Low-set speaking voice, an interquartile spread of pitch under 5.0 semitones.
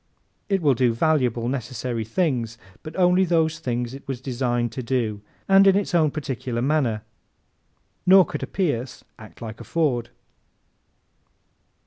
No: low, 130 Hz; average, 5.3 semitones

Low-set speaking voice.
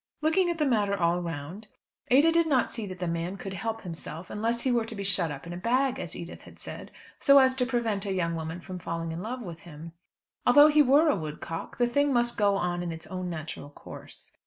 No: high, 200 Hz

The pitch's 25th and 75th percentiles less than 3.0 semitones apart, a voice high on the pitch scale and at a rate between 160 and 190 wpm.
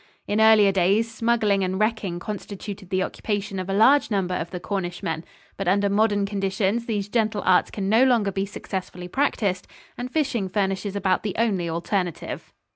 Yes: narrow, 2.5 semitones; high, 200 Hz; average, 170 wpm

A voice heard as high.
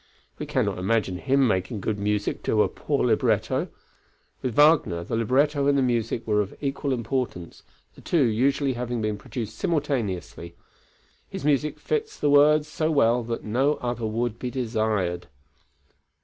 No: low, 120 Hz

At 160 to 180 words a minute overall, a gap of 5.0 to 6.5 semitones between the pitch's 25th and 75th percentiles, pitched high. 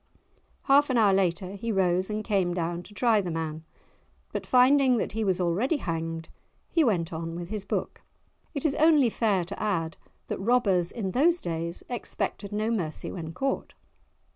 Yes: average, 175 wpm; wide, 5.6 semitones; high, 195 Hz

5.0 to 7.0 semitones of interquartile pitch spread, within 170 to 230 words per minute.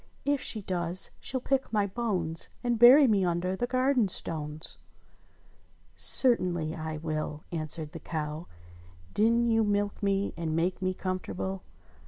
No: wide, 5.6 semitones; average, 145 wpm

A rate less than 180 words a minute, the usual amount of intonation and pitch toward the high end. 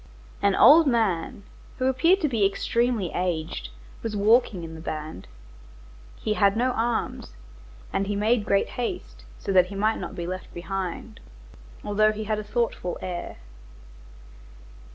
Yes: average, 150 wpm; average, 4.3 semitones; high, 205 Hz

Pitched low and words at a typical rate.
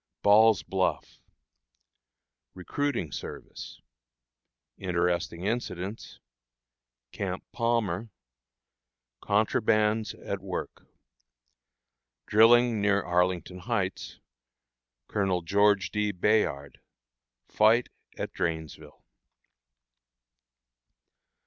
No: low, 100 Hz; slow, 60 wpm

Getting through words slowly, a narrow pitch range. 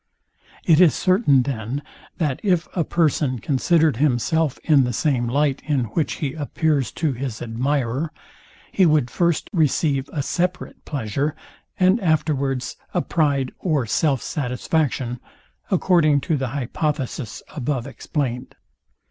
No: slow, 130 wpm; average, 3.8 semitones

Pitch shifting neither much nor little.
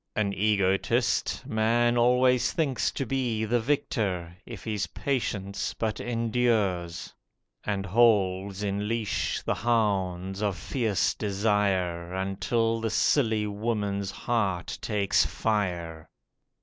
Yes: average, 3.3 semitones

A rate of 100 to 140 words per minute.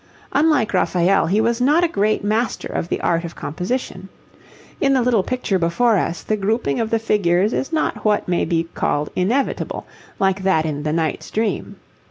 No: average, 185 wpm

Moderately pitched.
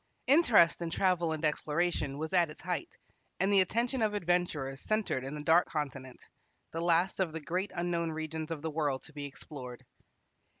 Yes: medium, 165 Hz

